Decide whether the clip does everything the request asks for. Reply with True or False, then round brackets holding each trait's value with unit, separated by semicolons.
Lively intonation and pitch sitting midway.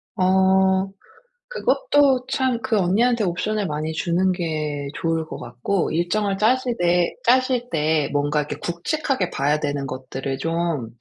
True (6.2 semitones; 175 Hz)